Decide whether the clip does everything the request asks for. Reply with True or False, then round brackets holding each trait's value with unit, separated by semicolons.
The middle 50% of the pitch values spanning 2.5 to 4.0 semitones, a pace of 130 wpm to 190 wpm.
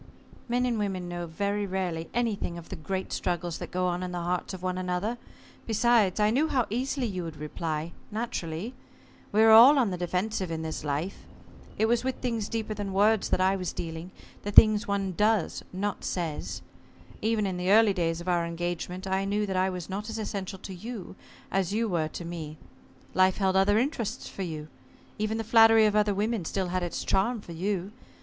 False (3.6 semitones; 205 wpm)